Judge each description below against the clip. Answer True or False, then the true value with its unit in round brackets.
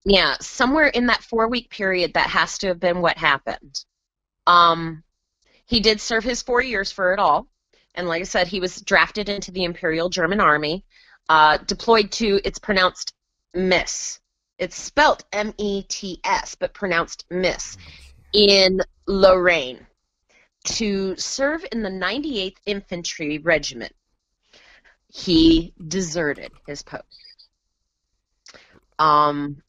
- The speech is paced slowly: True (130 wpm)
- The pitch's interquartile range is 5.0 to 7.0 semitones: False (4.2 semitones)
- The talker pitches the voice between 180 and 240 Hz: True (185 Hz)